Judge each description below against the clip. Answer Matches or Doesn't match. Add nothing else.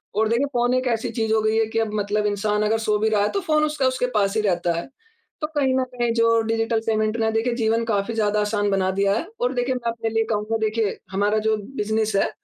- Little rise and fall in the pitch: Matches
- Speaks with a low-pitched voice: Doesn't match